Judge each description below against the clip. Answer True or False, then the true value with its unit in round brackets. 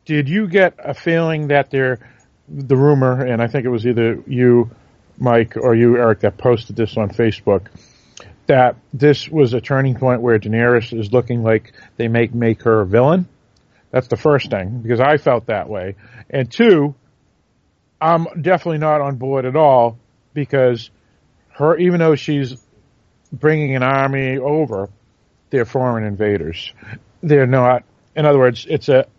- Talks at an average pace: True (160 wpm)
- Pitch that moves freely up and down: False (3.7 semitones)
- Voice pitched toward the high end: False (125 Hz)